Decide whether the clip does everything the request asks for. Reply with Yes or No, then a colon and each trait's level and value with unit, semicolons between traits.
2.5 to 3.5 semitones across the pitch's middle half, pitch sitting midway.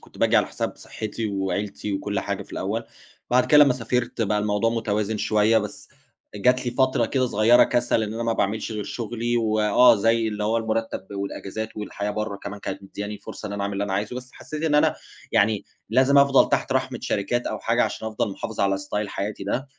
No: average, 2.8 semitones; low, 110 Hz